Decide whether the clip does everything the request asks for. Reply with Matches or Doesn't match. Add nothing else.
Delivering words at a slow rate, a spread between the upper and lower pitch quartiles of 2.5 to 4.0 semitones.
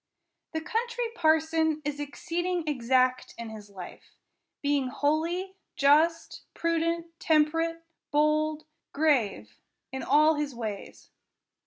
Matches